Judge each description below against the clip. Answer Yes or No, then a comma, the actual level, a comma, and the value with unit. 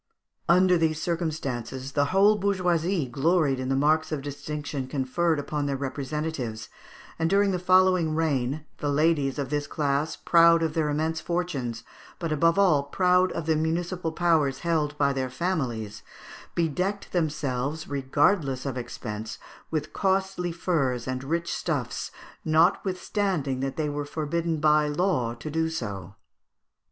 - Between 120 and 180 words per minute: Yes, average, 145 wpm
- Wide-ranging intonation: No, average, 3.8 semitones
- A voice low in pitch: No, medium, 155 Hz